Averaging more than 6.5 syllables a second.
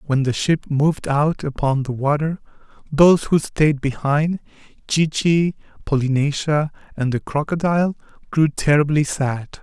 No: 4.5 syllables/s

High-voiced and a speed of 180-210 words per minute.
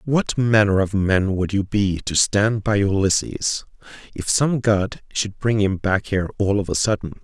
No: low, 100 Hz; average, 190 wpm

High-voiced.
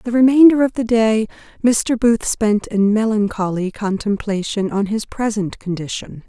Yes: high, 215 Hz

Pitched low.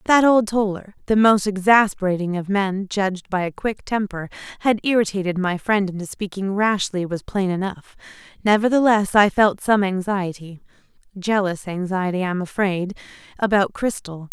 No: high, 195 Hz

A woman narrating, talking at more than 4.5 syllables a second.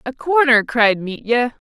No: female; 4.0 syllables/s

